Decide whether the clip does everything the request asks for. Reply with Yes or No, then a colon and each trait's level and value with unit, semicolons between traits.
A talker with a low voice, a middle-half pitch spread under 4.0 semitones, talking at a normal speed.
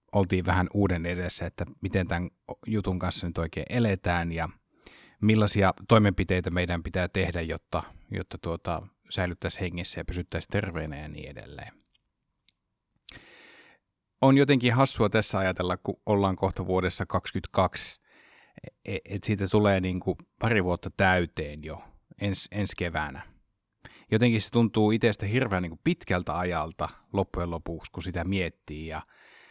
Yes: very low, 95 Hz; average, 2.7 semitones; average, 135 wpm